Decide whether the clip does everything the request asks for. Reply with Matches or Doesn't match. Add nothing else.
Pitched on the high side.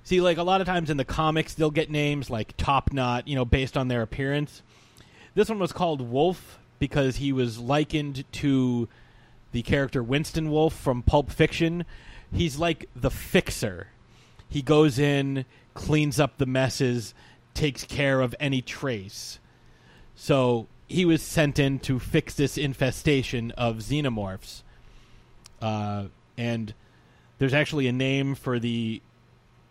Doesn't match